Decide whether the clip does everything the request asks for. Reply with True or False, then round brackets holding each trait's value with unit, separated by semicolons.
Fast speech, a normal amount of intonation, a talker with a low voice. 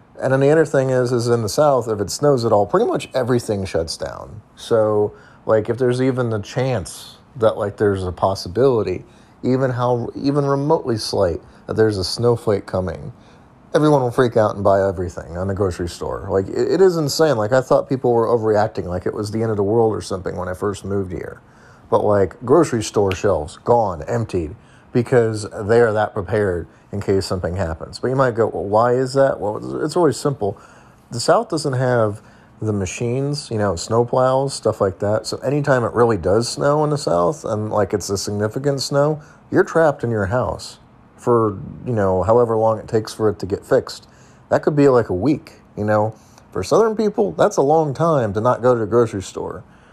True (210 wpm; 4.3 semitones; 115 Hz)